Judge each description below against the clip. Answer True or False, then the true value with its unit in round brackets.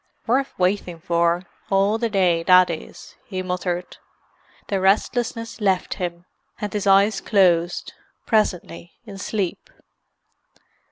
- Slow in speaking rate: True (115 wpm)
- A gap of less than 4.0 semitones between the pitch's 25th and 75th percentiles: True (2.9 semitones)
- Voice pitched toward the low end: False (190 Hz)